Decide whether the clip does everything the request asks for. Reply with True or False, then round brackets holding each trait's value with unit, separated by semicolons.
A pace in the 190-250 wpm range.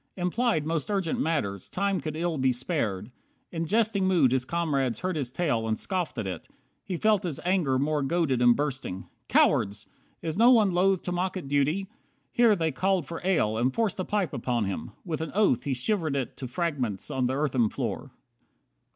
True (195 wpm)